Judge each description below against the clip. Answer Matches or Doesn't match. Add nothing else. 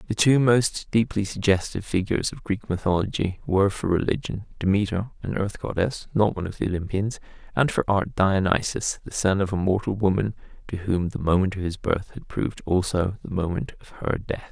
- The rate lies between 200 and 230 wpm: Doesn't match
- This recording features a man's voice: Matches